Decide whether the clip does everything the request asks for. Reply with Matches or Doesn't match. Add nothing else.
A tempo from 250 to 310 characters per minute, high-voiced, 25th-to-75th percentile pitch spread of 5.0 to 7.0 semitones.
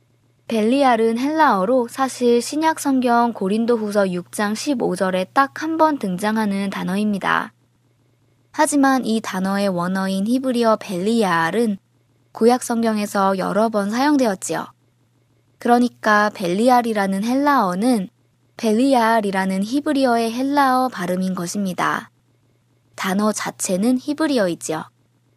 Matches